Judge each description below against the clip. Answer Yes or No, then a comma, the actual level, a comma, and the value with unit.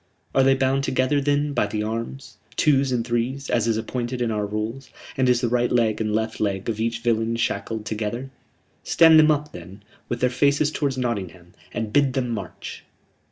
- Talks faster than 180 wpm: Yes, average, 195 wpm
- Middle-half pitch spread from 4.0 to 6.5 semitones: No, average, 3.5 semitones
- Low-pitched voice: Yes, low, 120 Hz